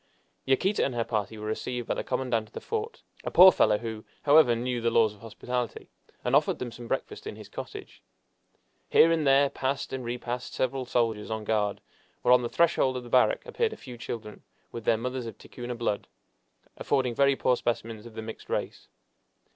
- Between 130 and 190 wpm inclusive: No, average, 200 wpm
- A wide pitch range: No, narrow, 2.6 semitones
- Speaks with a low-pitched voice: Yes, low, 120 Hz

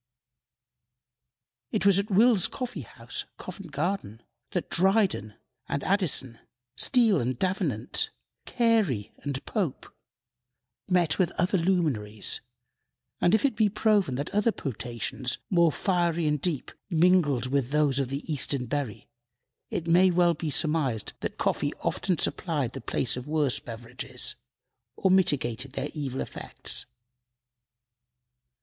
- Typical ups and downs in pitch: No, wide, 6.3 semitones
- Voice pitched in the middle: Yes, medium, 160 Hz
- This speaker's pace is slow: Yes, slow, 125 wpm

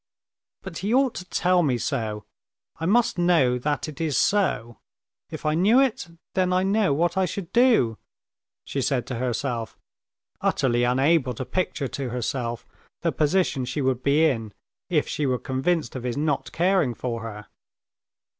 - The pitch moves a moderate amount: No, wide, 6.5 semitones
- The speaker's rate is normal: Yes, average, 165 wpm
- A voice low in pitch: No, medium, 145 Hz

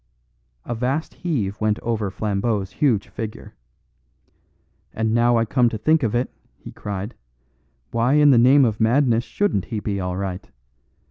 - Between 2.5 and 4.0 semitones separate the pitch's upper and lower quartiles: Yes, average, 3.3 semitones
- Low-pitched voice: Yes, low, 115 Hz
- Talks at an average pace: Yes, average, 155 wpm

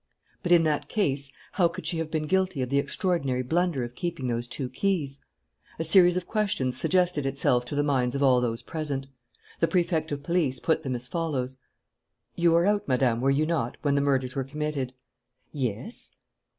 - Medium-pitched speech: Yes, medium, 145 Hz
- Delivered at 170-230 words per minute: Yes, average, 190 wpm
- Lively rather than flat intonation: No, average, 4.7 semitones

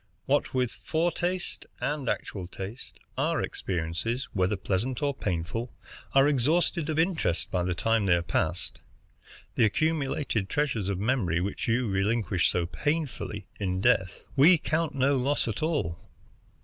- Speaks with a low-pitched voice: Yes, low, 115 Hz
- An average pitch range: No, wide, 7.5 semitones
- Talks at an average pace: Yes, average, 145 wpm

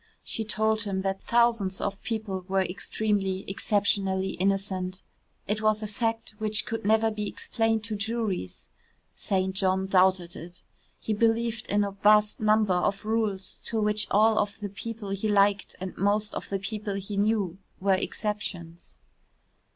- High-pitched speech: Yes, high, 205 Hz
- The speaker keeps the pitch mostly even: Yes, narrow, 2.2 semitones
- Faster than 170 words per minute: No, average, 155 wpm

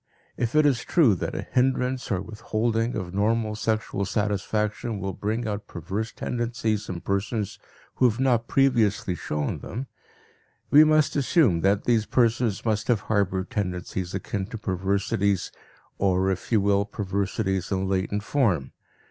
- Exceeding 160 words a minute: No, average, 150 wpm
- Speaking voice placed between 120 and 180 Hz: No, low, 105 Hz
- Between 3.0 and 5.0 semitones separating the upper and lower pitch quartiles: Yes, average, 3.3 semitones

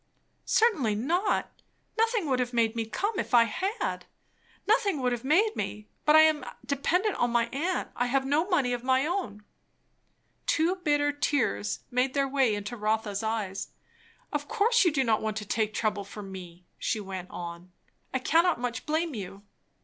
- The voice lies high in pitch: Yes, very high, 255 Hz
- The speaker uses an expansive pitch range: Yes, wide, 6.7 semitones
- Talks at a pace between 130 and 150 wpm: No, average, 175 wpm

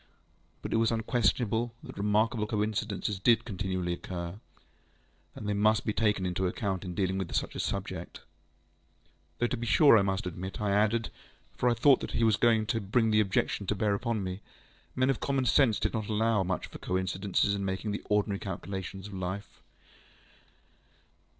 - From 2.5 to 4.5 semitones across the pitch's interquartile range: Yes, average, 2.8 semitones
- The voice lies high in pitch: No, low, 105 Hz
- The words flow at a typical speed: Yes, average, 185 wpm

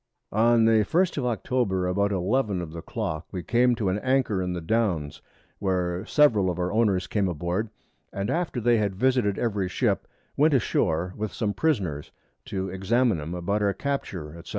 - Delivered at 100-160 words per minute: No, average, 185 wpm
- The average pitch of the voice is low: Yes, low, 100 Hz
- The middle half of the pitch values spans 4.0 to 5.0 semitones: Yes, average, 4.6 semitones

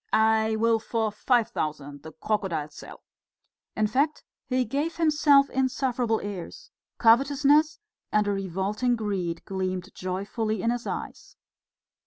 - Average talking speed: No, slow, 125 wpm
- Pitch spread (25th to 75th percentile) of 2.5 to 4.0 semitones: No, average, 5.0 semitones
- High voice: Yes, high, 220 Hz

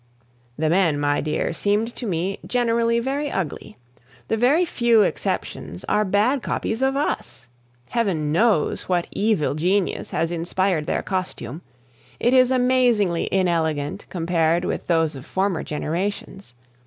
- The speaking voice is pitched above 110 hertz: Yes, high, 190 Hz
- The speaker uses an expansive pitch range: Yes, wide, 6.1 semitones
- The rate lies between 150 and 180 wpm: No, slow, 135 wpm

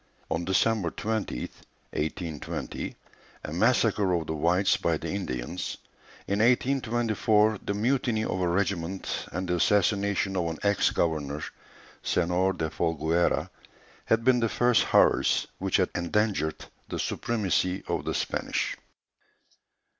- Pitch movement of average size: Yes, average, 4.3 semitones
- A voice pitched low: Yes, very low, 95 Hz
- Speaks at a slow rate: Yes, slow, 125 wpm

